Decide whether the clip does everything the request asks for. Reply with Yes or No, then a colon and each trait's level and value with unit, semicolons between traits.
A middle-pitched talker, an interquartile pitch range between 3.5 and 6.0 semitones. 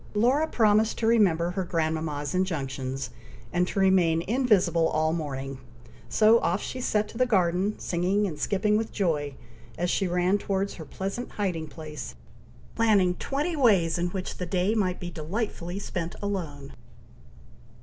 Yes: medium, 180 Hz; average, 4.4 semitones